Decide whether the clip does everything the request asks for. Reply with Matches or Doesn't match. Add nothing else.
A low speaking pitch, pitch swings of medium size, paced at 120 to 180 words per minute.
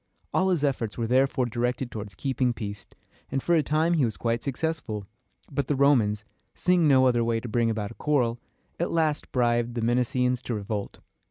Doesn't match